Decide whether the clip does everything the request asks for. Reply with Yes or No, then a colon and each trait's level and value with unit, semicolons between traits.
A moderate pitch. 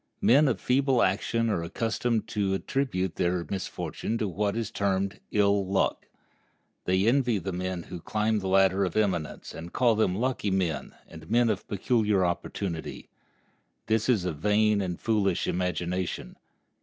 No: low, 100 Hz